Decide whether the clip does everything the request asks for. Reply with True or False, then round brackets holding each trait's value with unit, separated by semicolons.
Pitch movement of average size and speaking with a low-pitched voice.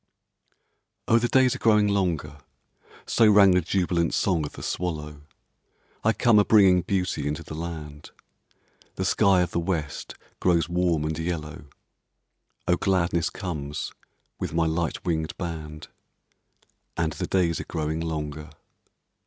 True (3.3 semitones; 85 Hz)